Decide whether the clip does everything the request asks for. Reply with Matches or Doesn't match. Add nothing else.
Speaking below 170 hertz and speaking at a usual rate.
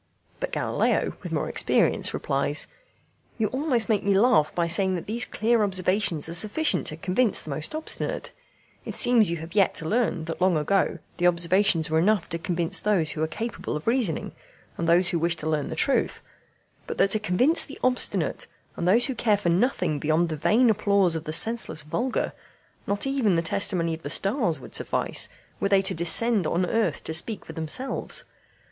Doesn't match